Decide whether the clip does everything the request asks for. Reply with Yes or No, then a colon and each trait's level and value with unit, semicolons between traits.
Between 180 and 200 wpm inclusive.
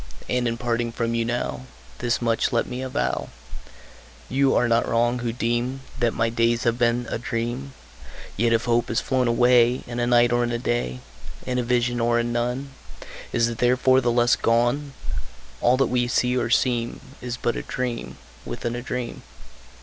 Yes: average, 190 wpm